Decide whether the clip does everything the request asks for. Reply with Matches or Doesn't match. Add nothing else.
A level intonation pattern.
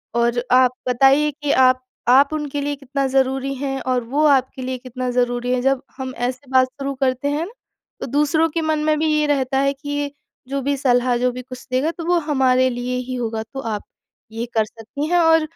Matches